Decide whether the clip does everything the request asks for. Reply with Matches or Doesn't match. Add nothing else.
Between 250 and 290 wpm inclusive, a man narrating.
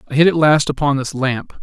Matches